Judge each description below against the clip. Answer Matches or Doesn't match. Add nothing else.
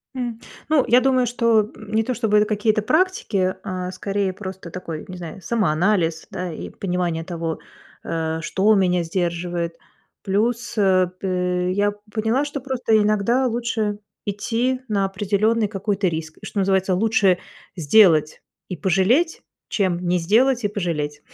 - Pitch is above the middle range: Matches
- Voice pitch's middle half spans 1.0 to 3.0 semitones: Doesn't match